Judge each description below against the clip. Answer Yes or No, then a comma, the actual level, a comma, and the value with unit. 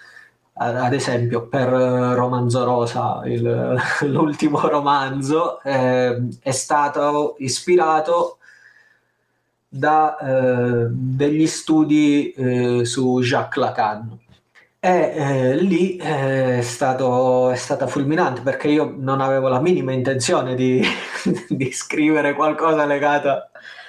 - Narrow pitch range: No, average, 3.2 semitones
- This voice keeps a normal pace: No, slow, 105 wpm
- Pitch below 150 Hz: Yes, low, 135 Hz